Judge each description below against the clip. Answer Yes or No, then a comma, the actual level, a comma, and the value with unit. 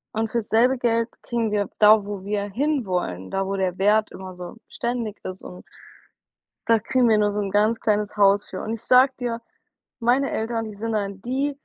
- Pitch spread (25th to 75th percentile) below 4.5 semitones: Yes, average, 2.8 semitones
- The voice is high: Yes, high, 215 Hz